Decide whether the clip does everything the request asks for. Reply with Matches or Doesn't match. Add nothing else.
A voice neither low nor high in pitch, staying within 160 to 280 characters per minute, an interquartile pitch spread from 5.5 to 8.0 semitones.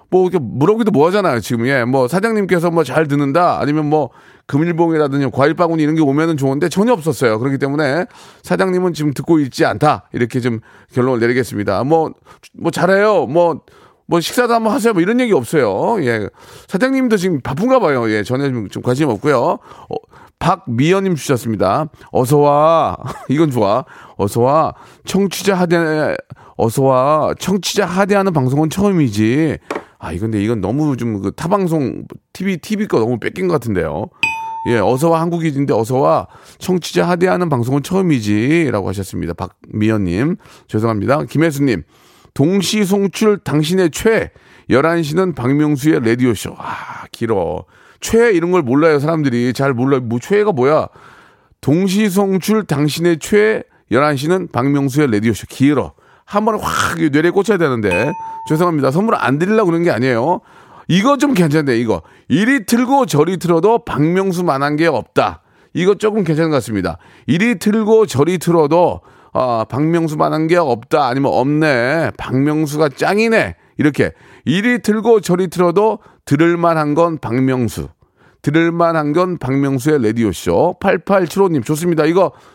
Doesn't match